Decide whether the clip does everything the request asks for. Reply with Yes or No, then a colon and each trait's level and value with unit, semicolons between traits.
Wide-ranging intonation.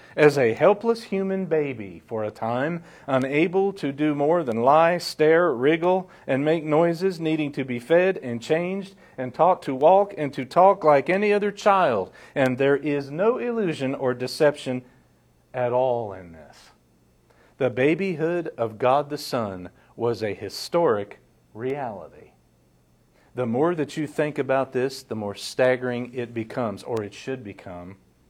Yes: wide, 6.1 semitones